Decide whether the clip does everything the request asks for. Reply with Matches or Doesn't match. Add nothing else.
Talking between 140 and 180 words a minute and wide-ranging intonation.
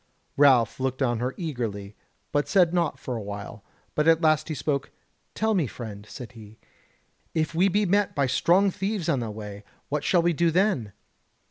Doesn't match